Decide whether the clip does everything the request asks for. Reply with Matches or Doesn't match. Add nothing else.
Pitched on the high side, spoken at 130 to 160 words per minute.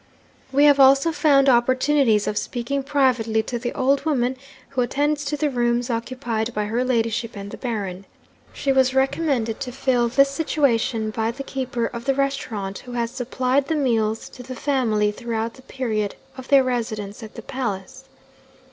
Doesn't match